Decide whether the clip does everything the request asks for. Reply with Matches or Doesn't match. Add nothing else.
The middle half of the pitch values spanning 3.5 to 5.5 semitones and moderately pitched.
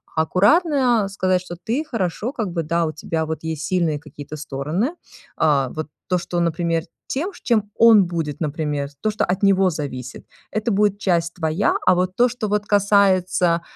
Matches